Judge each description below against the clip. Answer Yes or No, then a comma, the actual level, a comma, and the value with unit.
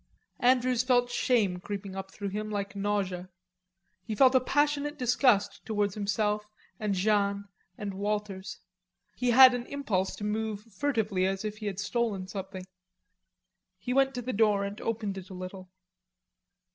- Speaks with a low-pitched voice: No, high, 210 Hz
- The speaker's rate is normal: Yes, average, 155 wpm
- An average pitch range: Yes, average, 3.7 semitones